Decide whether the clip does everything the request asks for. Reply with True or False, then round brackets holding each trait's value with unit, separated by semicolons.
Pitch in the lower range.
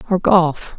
False (175 Hz)